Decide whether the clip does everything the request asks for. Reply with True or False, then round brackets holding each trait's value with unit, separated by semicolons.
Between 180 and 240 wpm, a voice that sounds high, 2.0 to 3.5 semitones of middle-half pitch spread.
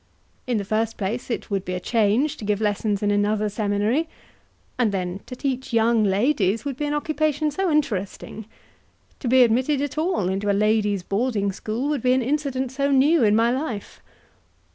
False (185 wpm; 230 Hz; 5.0 semitones)